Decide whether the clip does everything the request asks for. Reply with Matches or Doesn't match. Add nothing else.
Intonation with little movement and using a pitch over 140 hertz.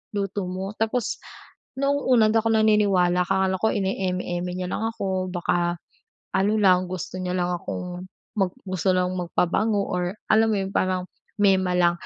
Matches